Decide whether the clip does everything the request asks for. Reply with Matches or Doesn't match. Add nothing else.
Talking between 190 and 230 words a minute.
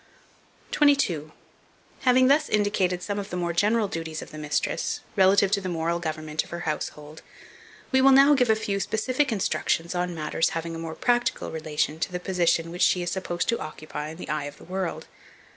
Matches